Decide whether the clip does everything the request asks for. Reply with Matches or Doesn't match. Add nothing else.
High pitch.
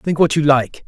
Doesn't match